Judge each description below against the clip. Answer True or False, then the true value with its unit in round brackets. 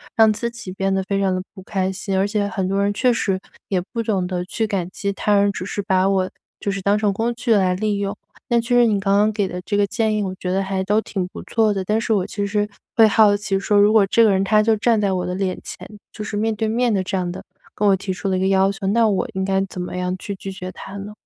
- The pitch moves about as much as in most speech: False (1.9 semitones)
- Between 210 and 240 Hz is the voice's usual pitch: False (200 Hz)